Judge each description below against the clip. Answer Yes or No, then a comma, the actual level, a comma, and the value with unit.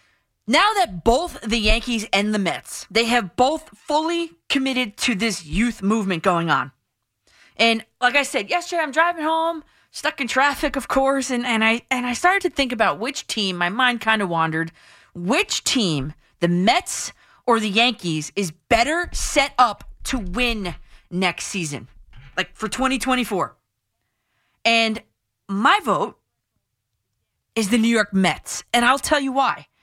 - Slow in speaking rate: No, average, 160 wpm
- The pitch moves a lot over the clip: Yes, wide, 6.6 semitones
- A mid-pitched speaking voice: No, high, 230 Hz